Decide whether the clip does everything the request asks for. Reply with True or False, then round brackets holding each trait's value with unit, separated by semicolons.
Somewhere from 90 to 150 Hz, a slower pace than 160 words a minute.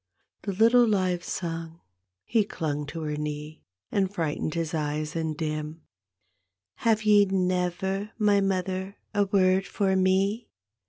False (180 Hz; 150 wpm)